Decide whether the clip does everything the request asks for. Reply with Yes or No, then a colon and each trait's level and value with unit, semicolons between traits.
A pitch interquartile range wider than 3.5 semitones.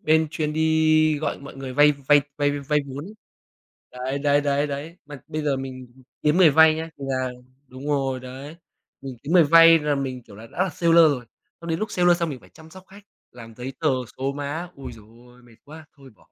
No: average, 3.2 semitones